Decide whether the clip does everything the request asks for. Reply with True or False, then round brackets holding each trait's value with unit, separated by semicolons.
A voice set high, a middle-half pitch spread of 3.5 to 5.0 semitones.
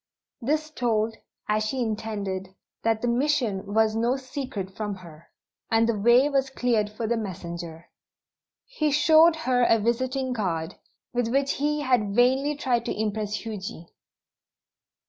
True (230 Hz; 4.1 semitones)